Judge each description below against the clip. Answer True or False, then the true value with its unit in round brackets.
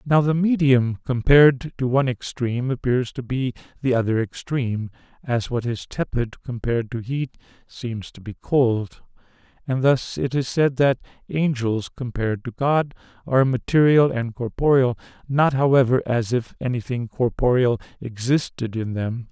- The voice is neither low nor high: False (125 Hz)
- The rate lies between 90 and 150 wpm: True (145 wpm)